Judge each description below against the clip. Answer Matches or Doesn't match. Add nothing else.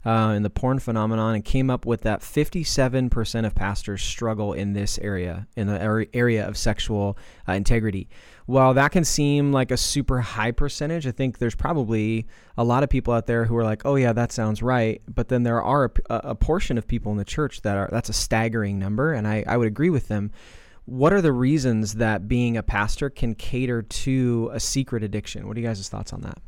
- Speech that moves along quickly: Matches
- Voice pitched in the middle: Doesn't match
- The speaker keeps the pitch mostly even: Doesn't match